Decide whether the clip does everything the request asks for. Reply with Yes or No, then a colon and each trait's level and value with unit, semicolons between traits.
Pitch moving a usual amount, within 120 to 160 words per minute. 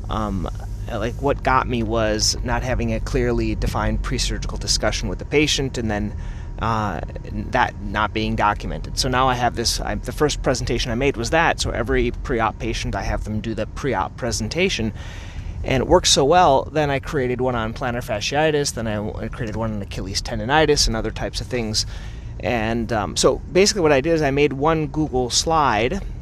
No: average, 3.7 semitones; average, 200 wpm